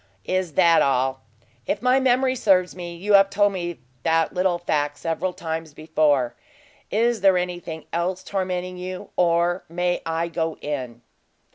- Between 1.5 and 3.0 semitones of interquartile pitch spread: Yes, narrow, 2.6 semitones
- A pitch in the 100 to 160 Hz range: No, medium, 175 Hz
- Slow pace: No, average, 150 wpm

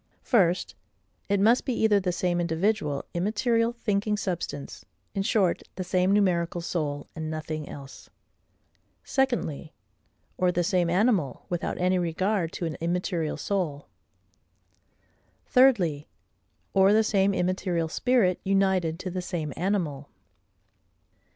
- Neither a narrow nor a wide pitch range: Yes, average, 3.5 semitones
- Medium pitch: Yes, medium, 180 Hz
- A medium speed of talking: No, slow, 120 wpm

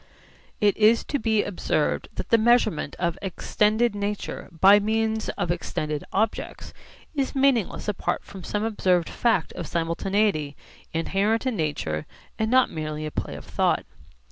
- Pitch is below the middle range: No, high, 205 Hz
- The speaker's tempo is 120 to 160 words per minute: Yes, average, 145 wpm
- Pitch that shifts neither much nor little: Yes, average, 4.7 semitones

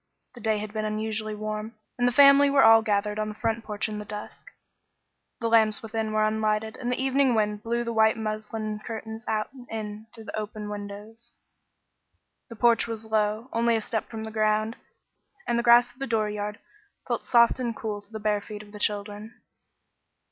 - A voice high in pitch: Yes, high, 220 Hz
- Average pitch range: No, narrow, 1.5 semitones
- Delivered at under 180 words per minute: No, average, 200 wpm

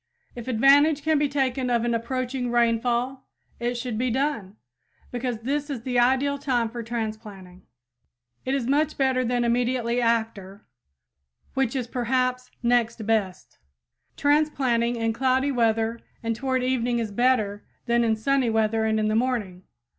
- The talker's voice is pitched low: No, high, 240 Hz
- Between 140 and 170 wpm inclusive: Yes, average, 150 wpm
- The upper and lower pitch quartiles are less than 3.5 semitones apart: Yes, narrow, 2.4 semitones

